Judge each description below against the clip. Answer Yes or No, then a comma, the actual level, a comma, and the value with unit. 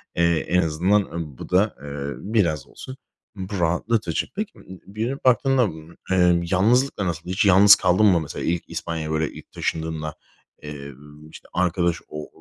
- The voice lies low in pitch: Yes, very low, 90 Hz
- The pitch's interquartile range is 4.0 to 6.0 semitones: Yes, average, 4.3 semitones